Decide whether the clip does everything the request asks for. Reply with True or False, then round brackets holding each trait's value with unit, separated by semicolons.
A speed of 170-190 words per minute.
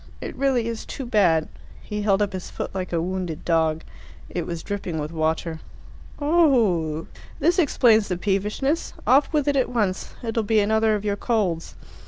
True (175 wpm)